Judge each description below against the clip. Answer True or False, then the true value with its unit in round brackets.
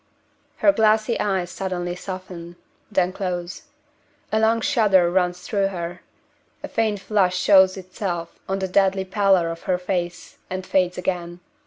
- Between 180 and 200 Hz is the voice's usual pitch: True (185 Hz)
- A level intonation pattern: True (1.8 semitones)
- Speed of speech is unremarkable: True (145 wpm)